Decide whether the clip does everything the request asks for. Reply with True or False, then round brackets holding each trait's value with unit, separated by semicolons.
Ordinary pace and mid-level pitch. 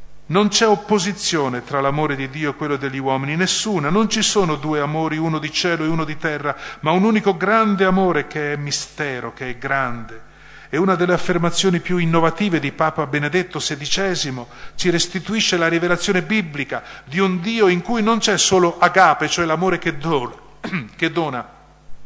False (175 wpm; 165 Hz)